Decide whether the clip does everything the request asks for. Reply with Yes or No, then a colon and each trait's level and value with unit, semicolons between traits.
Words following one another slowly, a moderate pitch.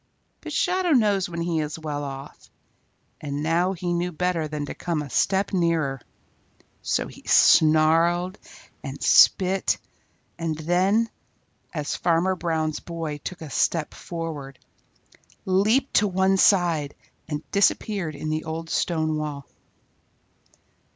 Yes: slow, 130 wpm; medium, 165 Hz